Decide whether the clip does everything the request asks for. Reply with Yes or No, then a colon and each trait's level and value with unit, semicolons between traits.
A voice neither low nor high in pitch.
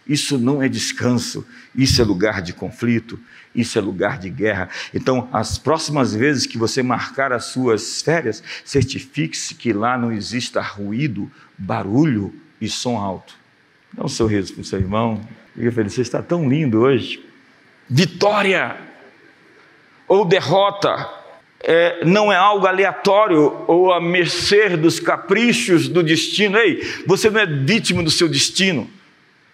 Yes: medium, 145 Hz